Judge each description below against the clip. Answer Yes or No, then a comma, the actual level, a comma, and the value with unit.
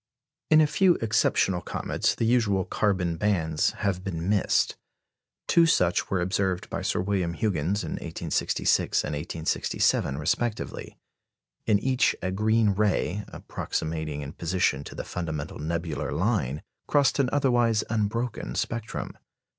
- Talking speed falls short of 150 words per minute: Yes, slow, 135 wpm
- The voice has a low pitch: Yes, very low, 95 Hz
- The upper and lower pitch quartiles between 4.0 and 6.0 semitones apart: Yes, average, 5.2 semitones